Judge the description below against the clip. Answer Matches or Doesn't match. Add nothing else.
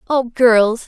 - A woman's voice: Matches